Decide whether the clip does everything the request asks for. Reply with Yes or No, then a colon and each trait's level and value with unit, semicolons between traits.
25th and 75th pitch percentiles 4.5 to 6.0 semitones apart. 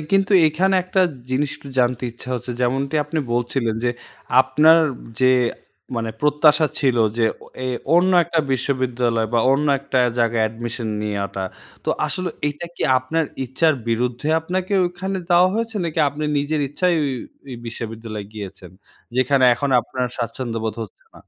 Yes: average, 5.1 semitones